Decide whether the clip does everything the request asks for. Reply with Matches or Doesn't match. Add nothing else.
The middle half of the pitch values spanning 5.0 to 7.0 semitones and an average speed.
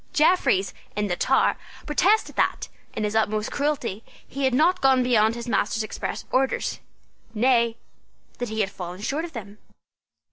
Doesn't match